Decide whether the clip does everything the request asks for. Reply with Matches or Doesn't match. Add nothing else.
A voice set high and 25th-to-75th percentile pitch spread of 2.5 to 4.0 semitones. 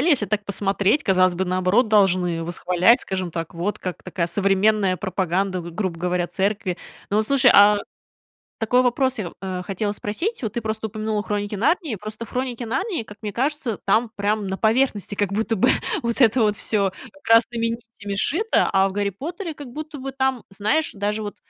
Matches